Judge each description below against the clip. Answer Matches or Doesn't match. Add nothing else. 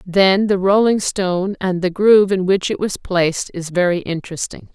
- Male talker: Doesn't match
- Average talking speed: Matches